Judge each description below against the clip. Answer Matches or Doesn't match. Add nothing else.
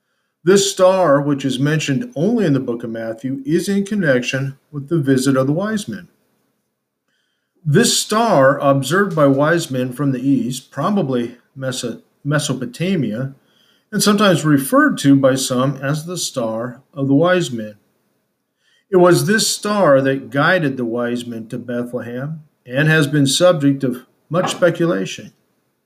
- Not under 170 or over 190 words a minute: Doesn't match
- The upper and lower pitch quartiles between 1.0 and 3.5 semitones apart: Doesn't match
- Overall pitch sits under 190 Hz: Matches